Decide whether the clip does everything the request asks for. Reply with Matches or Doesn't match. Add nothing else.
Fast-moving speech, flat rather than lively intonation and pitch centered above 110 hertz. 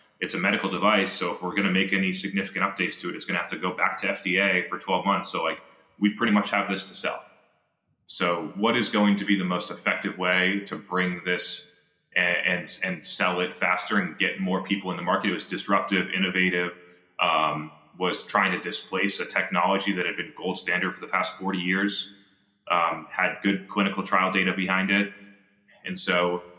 Doesn't match